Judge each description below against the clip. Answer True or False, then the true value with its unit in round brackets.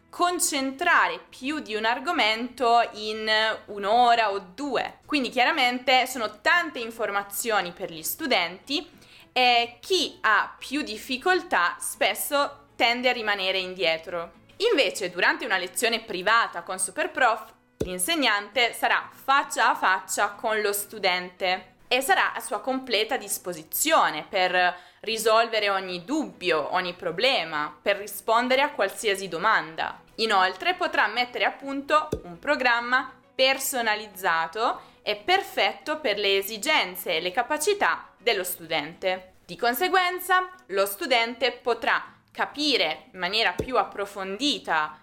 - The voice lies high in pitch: True (230 Hz)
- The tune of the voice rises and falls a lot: True (6.2 semitones)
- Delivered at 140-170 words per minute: False (115 wpm)